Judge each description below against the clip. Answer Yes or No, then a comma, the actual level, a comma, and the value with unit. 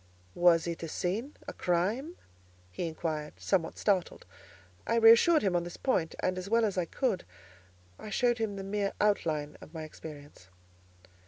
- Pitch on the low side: No, medium, 185 Hz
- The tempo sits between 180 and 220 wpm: No, average, 165 wpm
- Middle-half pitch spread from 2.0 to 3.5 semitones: No, average, 5.0 semitones